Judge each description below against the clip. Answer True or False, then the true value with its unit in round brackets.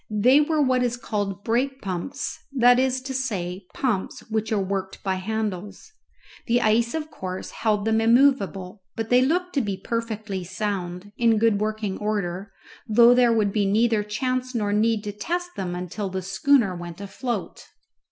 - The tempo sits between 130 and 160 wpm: False (170 wpm)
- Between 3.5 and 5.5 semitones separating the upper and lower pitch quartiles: True (4.0 semitones)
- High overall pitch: True (215 Hz)